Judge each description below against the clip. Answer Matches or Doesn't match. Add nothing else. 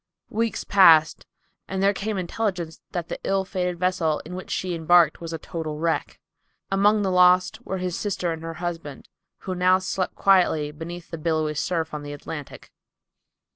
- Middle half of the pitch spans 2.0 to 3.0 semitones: Matches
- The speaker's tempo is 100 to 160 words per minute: Doesn't match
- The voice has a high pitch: Doesn't match